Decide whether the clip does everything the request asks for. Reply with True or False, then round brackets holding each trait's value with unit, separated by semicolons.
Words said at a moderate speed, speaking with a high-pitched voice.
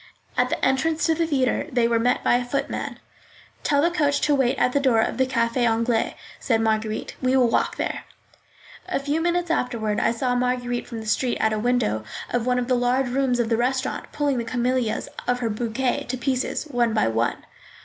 False (210 wpm; 245 Hz)